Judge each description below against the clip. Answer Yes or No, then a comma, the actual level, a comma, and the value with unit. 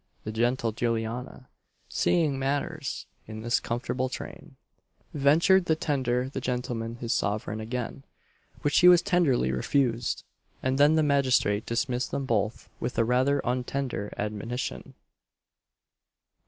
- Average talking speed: No, slow, 125 wpm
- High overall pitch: No, low, 125 Hz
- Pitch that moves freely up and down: No, average, 3.5 semitones